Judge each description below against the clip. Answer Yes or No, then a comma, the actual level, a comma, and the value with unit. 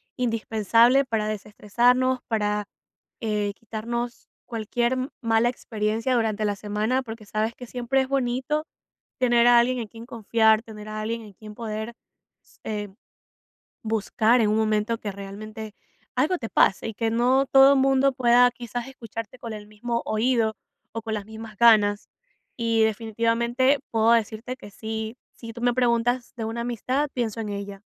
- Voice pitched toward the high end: Yes, high, 230 Hz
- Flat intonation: Yes, narrow, 2.2 semitones